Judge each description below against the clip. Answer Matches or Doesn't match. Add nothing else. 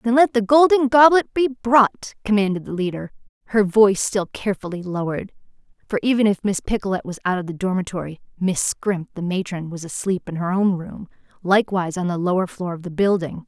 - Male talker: Doesn't match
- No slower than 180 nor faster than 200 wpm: Matches